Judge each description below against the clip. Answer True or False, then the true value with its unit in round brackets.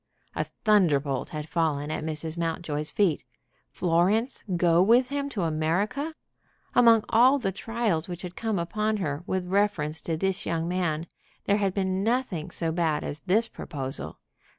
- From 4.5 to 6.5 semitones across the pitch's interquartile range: True (5.0 semitones)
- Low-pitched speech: False (180 Hz)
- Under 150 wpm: False (160 wpm)